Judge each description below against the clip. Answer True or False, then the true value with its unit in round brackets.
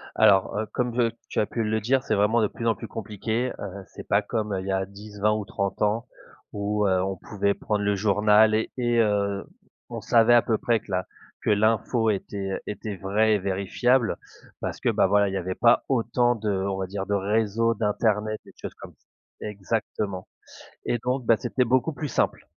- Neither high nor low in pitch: False (105 Hz)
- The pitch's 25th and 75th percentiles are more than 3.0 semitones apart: False (2.4 semitones)